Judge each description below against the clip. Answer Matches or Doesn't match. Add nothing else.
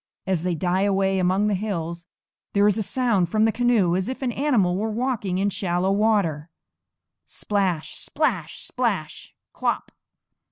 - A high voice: Matches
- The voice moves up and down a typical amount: Matches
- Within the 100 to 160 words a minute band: Matches